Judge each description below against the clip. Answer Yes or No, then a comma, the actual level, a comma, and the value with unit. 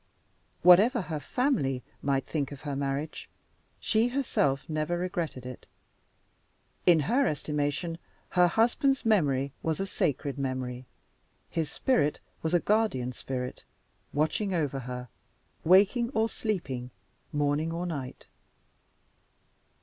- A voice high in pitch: No, medium, 155 Hz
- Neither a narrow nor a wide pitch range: No, wide, 6.0 semitones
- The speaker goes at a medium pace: No, slow, 115 wpm